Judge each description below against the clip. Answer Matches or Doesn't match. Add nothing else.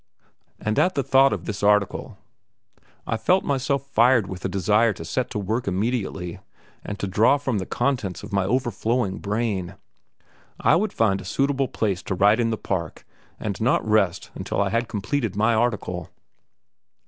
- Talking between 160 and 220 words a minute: Matches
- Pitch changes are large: Doesn't match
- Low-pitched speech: Matches